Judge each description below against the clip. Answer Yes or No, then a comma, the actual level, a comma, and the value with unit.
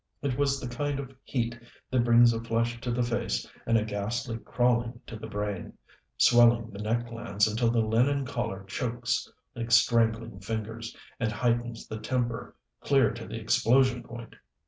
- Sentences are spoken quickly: No, average, 170 wpm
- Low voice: Yes, low, 115 Hz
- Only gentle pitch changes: Yes, narrow, 1.3 semitones